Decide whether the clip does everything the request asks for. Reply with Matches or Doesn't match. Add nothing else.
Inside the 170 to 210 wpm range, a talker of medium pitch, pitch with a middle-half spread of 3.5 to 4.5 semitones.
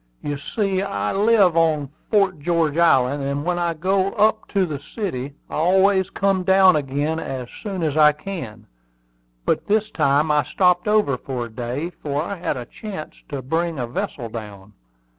Doesn't match